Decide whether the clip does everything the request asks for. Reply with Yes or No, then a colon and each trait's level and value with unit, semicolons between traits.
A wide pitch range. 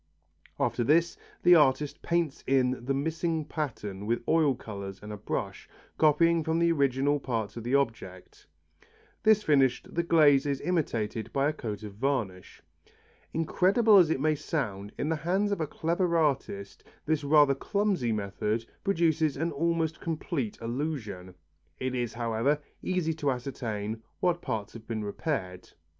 Yes: wide, 6.1 semitones